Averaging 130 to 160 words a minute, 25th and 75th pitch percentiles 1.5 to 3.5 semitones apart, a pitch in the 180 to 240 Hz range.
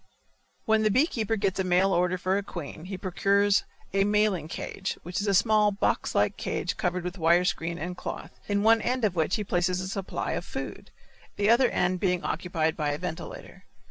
No: fast, 205 wpm; narrow, 2.6 semitones; high, 190 Hz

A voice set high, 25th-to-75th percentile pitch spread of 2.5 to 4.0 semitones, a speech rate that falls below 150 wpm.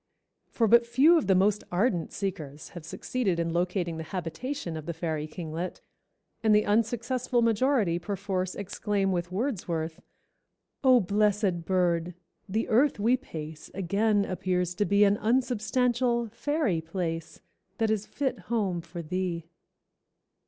No: high, 195 Hz; average, 5.1 semitones; average, 140 wpm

